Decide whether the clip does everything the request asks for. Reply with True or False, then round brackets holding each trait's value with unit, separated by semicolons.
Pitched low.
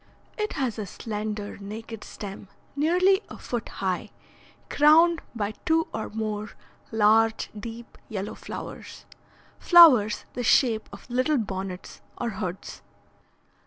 False (225 Hz)